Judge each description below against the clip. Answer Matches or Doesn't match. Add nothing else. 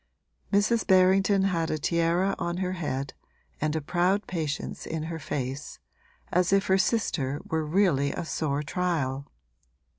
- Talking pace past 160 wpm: Doesn't match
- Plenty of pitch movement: Doesn't match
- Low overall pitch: Doesn't match